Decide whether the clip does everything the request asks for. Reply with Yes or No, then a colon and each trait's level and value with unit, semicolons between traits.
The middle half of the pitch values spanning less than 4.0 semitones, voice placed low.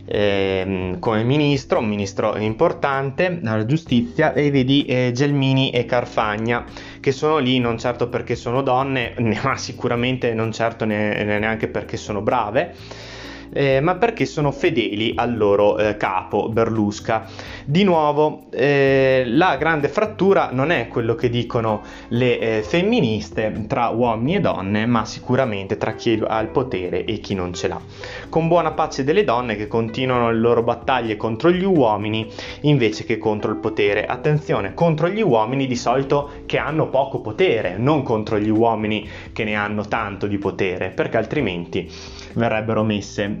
No: average, 4.3 semitones; low, 120 Hz